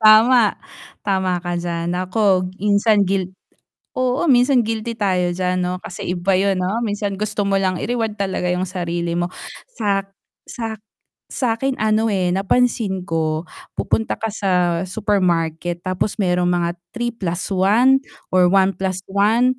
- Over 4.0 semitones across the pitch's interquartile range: No, average, 3.4 semitones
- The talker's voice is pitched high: Yes, high, 195 Hz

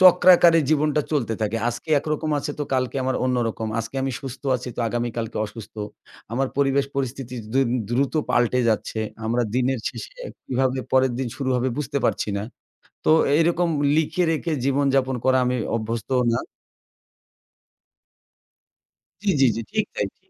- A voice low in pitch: Yes, low, 130 Hz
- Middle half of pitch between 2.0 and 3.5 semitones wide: Yes, average, 3.1 semitones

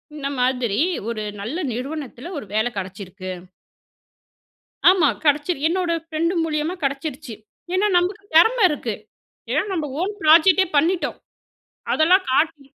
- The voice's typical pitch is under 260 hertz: No, very high, 305 Hz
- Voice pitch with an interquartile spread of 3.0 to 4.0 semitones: No, wide, 5.5 semitones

